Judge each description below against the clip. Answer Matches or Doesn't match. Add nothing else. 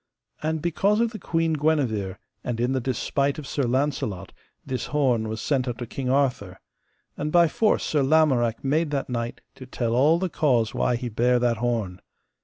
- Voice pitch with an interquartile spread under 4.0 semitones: Doesn't match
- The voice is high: Doesn't match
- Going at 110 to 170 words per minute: Doesn't match